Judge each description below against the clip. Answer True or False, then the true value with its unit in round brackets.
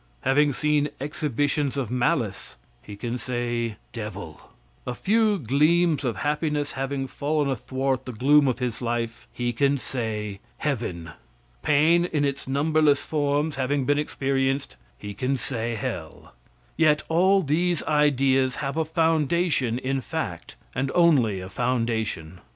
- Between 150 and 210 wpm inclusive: False (135 wpm)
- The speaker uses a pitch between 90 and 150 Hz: True (135 Hz)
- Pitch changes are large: False (3.8 semitones)